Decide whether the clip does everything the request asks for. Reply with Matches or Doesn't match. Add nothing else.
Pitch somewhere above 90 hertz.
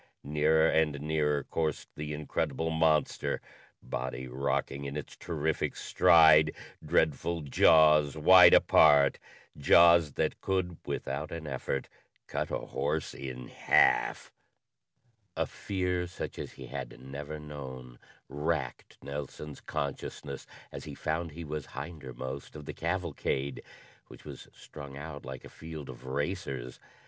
Doesn't match